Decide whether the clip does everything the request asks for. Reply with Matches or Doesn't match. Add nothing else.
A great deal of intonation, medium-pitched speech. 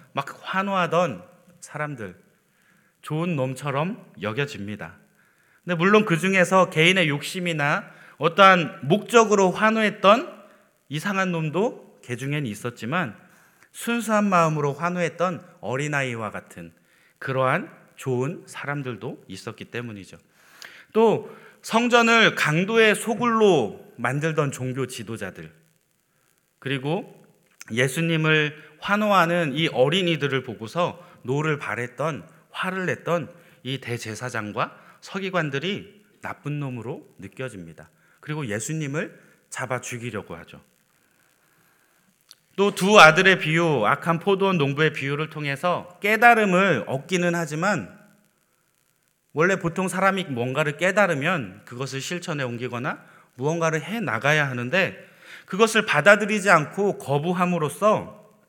Matches